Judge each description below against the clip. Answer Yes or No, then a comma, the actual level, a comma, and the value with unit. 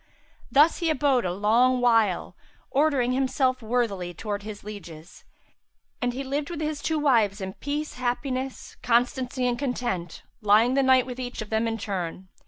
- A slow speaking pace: No, average, 165 wpm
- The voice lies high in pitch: Yes, high, 245 Hz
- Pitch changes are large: No, average, 4.2 semitones